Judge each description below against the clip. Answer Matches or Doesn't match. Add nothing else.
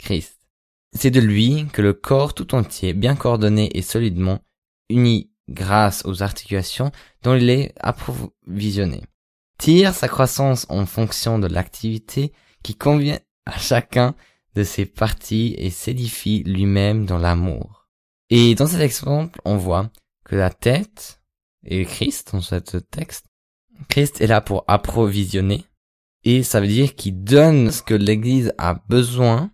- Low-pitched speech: Matches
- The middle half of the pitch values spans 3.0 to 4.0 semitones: Doesn't match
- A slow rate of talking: Matches